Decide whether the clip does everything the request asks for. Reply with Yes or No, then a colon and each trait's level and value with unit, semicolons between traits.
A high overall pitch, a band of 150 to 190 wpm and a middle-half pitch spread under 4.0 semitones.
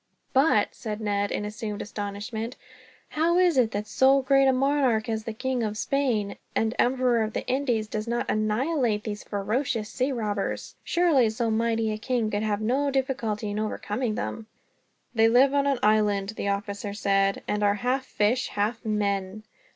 Yes: high, 220 Hz; average, 175 wpm; average, 3.6 semitones